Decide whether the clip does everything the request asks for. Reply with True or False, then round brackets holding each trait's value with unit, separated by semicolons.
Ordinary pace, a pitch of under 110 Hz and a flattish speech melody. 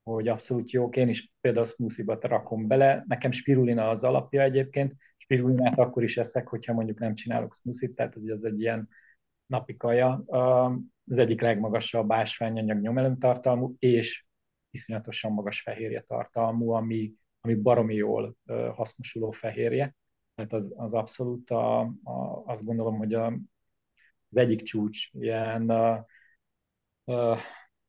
False (135 wpm; 115 Hz; 1.9 semitones)